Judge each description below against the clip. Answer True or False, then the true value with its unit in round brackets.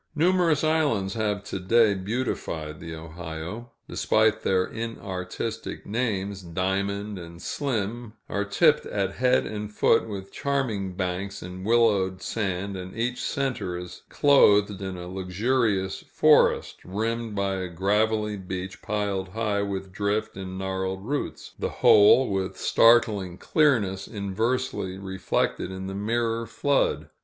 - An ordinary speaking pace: False (130 wpm)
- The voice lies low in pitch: True (100 Hz)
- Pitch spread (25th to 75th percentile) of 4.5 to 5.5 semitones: False (3.4 semitones)